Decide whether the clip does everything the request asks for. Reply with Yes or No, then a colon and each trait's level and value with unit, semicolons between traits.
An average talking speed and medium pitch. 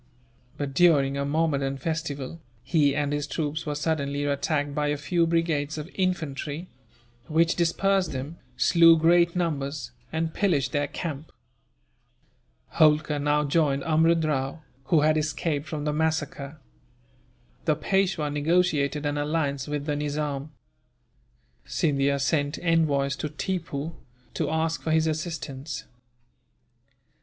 No: slow, 125 wpm; medium, 150 Hz